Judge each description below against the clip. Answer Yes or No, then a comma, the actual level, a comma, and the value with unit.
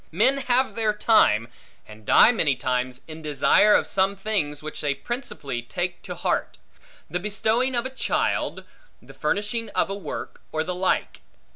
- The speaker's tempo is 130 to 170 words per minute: Yes, average, 165 wpm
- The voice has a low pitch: No, high, 190 Hz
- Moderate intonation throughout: No, wide, 7.3 semitones